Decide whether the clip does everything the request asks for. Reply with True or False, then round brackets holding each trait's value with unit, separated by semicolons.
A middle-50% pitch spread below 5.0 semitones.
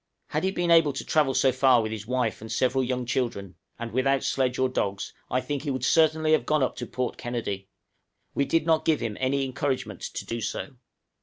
True (3.2 semitones)